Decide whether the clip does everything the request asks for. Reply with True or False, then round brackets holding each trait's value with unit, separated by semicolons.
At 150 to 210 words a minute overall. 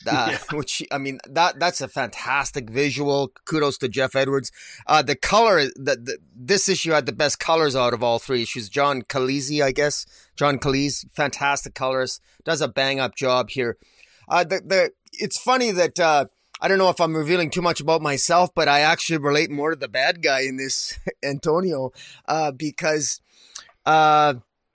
True (180 wpm)